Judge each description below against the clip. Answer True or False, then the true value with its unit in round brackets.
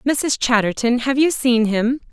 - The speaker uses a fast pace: False (170 wpm)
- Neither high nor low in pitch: False (245 Hz)